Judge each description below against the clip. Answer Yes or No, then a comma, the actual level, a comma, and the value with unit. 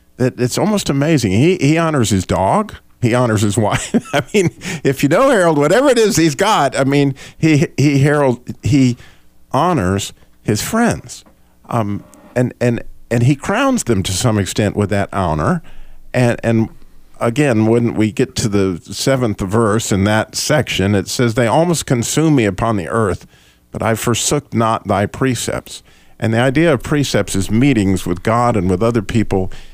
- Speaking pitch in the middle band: No, low, 120 Hz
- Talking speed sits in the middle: Yes, average, 175 wpm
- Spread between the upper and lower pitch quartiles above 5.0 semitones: Yes, wide, 5.5 semitones